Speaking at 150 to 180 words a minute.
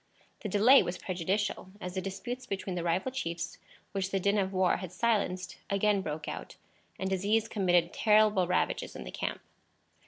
Yes: average, 175 wpm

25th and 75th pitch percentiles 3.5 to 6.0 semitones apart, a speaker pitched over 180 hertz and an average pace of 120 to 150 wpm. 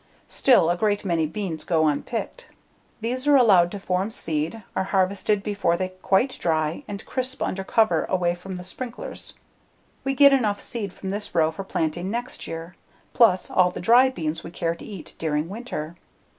No: average, 5.0 semitones; high, 190 Hz; average, 180 wpm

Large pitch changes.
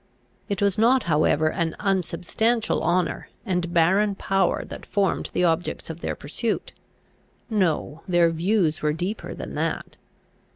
No: average, 3.7 semitones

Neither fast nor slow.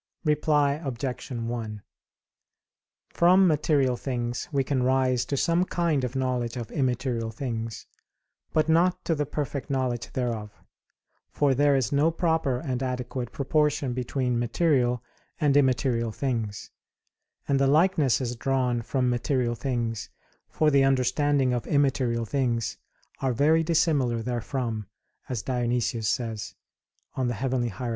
No: slow, 125 wpm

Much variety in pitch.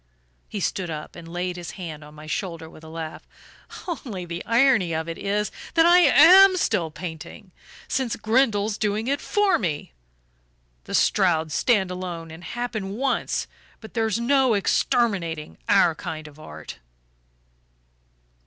Yes: wide, 6.2 semitones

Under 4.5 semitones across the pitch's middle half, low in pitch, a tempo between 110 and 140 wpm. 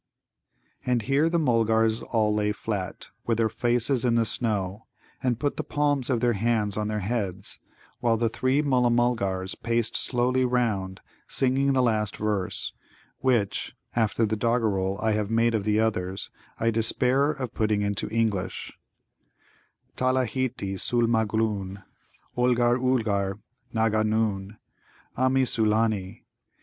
Yes: average, 2.8 semitones; low, 115 Hz; slow, 135 wpm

